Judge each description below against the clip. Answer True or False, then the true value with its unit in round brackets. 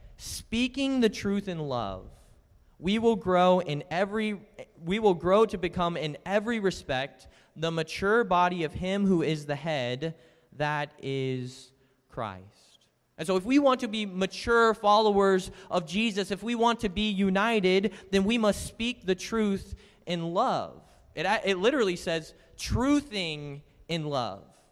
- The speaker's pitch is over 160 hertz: True (190 Hz)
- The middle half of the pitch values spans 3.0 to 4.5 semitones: False (5.3 semitones)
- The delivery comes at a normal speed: True (150 wpm)